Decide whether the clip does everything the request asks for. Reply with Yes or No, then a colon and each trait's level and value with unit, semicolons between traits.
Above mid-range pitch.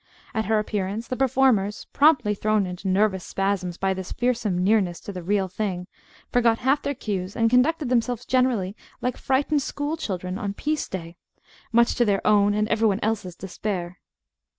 Yes: high, 210 Hz